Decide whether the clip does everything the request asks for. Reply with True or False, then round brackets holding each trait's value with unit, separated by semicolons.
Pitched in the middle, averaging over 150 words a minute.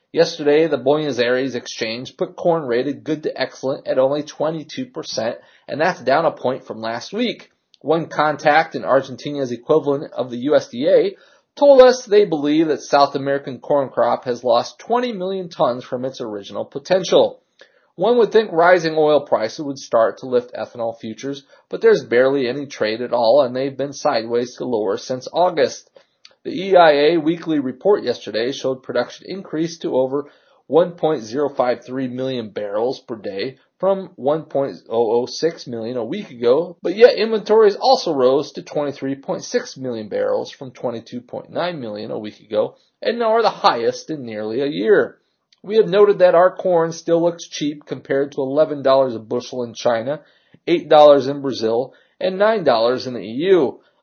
True (150 Hz; 160 wpm)